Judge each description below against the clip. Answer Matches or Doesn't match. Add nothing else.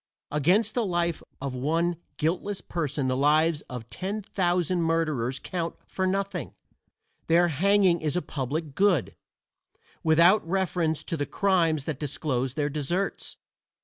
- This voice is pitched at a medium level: Matches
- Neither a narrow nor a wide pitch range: Matches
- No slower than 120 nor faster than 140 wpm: Matches